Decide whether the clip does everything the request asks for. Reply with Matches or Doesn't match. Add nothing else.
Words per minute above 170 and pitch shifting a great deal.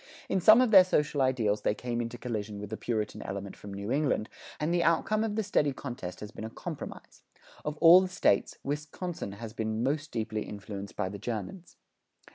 Matches